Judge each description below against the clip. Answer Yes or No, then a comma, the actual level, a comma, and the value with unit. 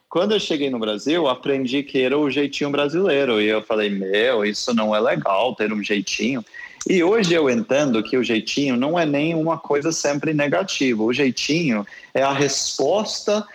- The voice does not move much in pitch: No, average, 4.9 semitones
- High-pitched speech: No, low, 135 Hz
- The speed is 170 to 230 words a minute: Yes, average, 180 wpm